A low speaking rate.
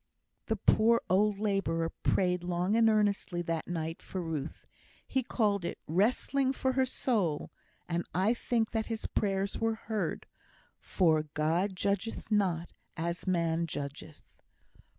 Yes: slow, 130 wpm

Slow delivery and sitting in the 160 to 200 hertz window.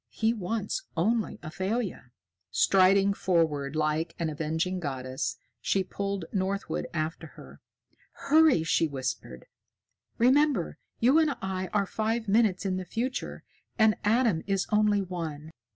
Yes: slow, 125 wpm; high, 190 Hz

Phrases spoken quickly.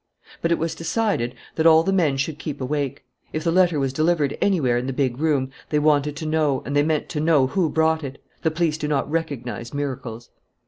Yes: fast, 220 wpm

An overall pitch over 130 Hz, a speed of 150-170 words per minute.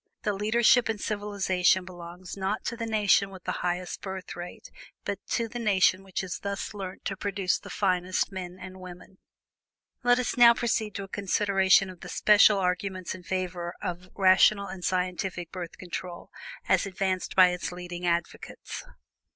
Yes: high, 190 Hz; average, 165 wpm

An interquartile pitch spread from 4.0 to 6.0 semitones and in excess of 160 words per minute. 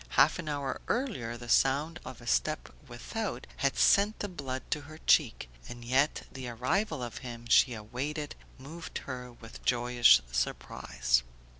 No: average, 4.3 semitones; average, 155 wpm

